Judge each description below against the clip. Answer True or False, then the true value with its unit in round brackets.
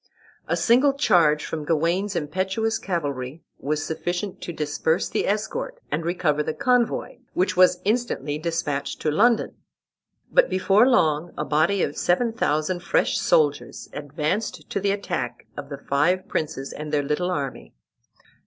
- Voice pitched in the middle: True (170 Hz)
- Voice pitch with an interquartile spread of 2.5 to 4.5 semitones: False (5.1 semitones)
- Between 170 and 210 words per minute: False (145 wpm)